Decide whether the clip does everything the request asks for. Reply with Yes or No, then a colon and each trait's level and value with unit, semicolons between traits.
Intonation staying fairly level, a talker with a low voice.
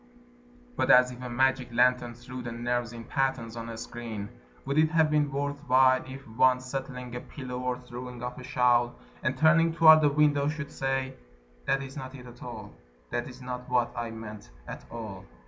Yes: narrow, 2.1 semitones; low, 125 Hz